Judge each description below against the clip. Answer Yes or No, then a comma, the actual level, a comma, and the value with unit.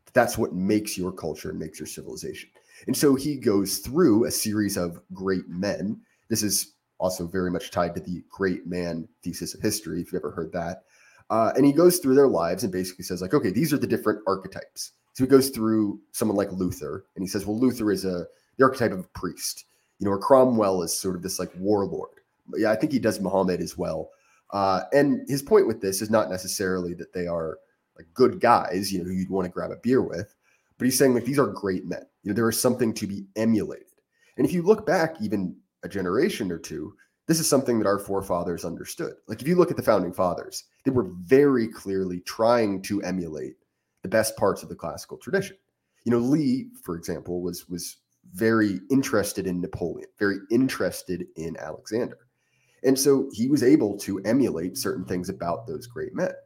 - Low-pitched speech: Yes, low, 105 Hz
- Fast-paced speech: Yes, fast, 210 wpm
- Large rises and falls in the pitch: Yes, wide, 6.1 semitones